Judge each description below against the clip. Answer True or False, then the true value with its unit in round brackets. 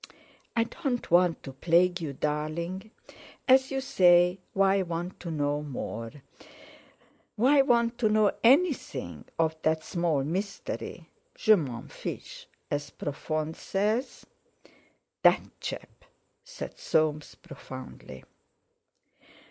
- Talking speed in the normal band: False (105 wpm)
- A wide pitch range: True (6.3 semitones)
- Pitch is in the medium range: True (175 Hz)